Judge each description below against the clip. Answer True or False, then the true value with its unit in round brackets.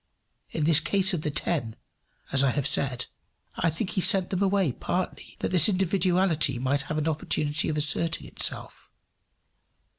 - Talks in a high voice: False (160 Hz)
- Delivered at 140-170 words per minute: True (160 wpm)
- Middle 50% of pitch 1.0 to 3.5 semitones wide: False (4.3 semitones)